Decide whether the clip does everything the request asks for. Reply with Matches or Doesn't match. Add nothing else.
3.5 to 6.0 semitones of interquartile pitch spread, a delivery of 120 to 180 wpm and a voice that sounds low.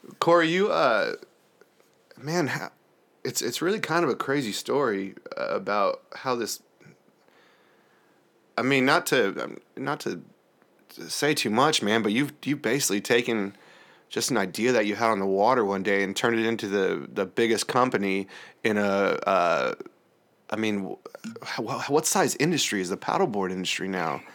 Doesn't match